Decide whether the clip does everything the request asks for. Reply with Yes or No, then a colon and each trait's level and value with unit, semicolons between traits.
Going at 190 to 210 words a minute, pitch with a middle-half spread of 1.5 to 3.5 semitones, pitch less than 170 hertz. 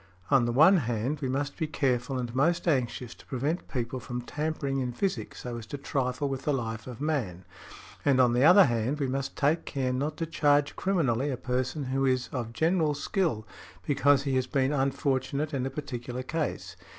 Yes: average, 200 wpm; average, 2.9 semitones; low, 135 Hz